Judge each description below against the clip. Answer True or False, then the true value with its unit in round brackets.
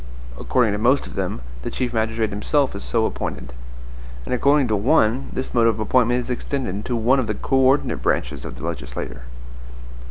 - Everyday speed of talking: True (190 wpm)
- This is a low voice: True (115 Hz)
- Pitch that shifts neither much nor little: True (3.5 semitones)